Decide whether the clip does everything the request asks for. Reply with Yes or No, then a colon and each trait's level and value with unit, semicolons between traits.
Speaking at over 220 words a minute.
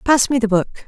Yes: fast, 275 wpm